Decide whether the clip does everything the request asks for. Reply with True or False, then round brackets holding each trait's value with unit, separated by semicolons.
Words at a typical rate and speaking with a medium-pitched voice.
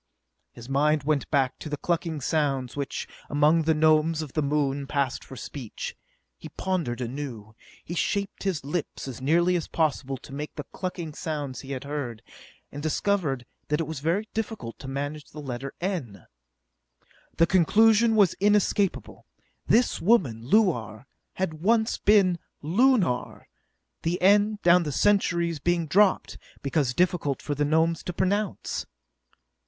True (150 wpm; 155 Hz)